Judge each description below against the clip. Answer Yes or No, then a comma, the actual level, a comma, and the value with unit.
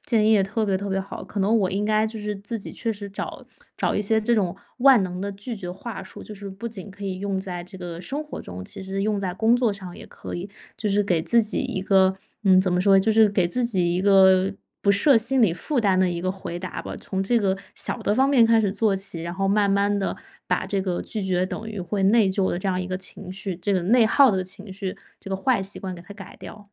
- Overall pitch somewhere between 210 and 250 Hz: No, high, 195 Hz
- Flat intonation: Yes, narrow, 2.3 semitones